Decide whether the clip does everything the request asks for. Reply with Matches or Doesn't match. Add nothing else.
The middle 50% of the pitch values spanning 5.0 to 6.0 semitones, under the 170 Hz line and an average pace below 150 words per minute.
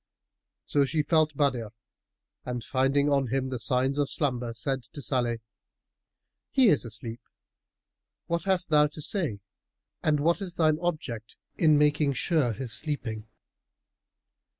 Doesn't match